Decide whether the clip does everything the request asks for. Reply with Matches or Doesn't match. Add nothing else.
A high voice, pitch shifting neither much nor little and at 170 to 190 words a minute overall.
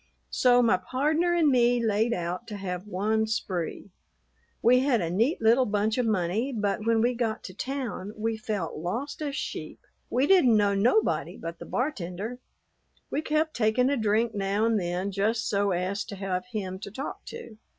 Matches